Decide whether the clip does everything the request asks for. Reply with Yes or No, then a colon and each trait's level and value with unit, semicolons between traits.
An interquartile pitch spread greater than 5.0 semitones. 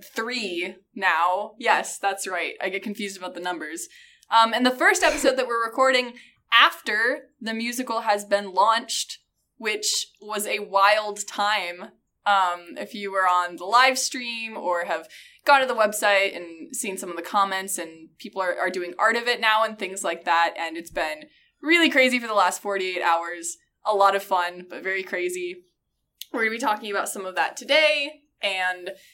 Yes: wide, 5.5 semitones